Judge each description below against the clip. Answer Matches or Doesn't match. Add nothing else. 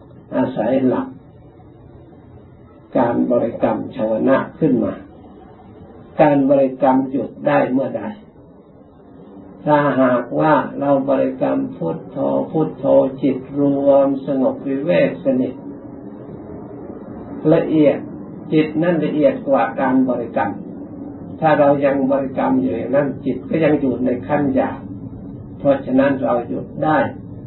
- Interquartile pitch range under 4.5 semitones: Doesn't match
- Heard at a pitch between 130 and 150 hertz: Matches